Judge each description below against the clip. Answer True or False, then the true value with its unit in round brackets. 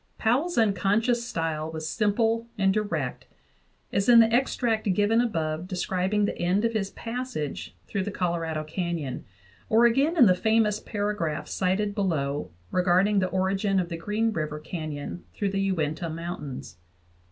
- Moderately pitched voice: False (195 Hz)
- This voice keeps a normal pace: True (150 wpm)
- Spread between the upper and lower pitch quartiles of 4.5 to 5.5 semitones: True (4.8 semitones)